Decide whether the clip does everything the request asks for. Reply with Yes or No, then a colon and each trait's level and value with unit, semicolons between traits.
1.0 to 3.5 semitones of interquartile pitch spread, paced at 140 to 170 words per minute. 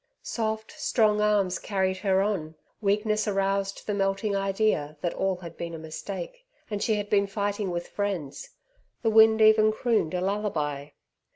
Yes: narrow, 2.4 semitones; average, 160 wpm